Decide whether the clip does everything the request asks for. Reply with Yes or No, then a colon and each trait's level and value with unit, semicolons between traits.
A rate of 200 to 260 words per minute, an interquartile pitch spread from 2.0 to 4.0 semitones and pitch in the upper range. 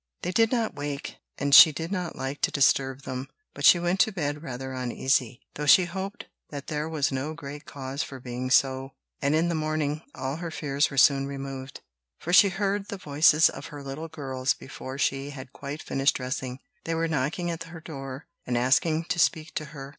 No: fast, 205 wpm; average, 3.3 semitones; medium, 145 Hz